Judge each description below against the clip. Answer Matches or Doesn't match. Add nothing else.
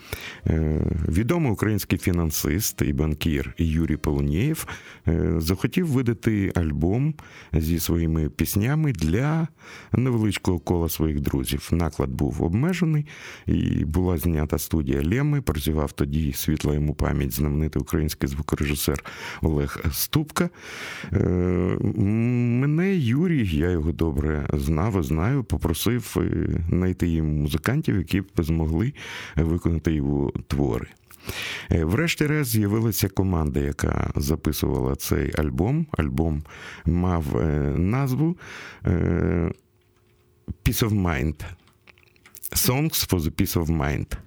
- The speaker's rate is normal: Doesn't match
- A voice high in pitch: Doesn't match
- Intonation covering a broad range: Matches